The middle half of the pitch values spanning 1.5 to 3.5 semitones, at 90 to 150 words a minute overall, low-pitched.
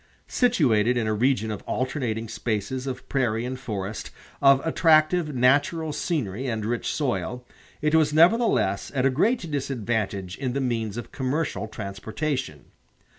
No: average, 5.1 semitones; average, 140 wpm; low, 125 Hz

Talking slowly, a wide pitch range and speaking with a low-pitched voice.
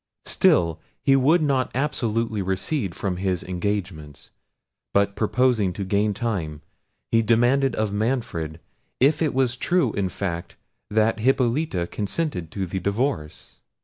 Yes: slow, 130 wpm; wide, 5.7 semitones; low, 105 Hz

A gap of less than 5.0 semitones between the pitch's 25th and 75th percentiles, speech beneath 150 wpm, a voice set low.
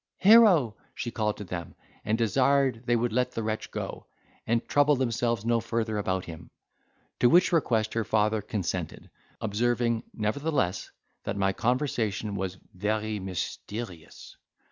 Yes: average, 2.8 semitones; average, 140 wpm; low, 110 Hz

